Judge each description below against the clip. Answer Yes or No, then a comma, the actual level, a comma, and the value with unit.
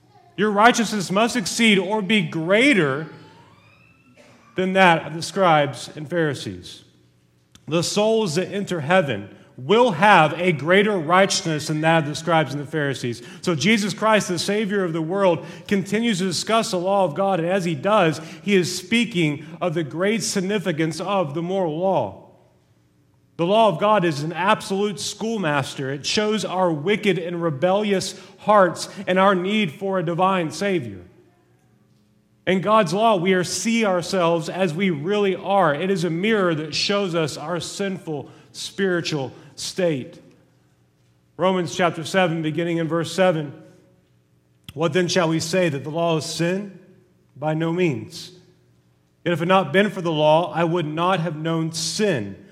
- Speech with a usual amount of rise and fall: Yes, average, 3.8 semitones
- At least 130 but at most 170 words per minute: Yes, average, 160 wpm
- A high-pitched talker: No, medium, 175 Hz